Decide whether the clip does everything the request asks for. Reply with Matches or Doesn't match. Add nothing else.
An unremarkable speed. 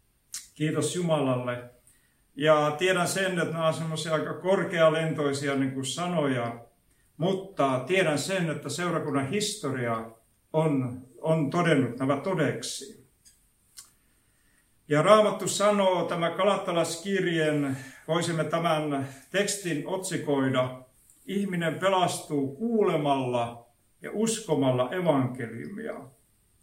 Doesn't match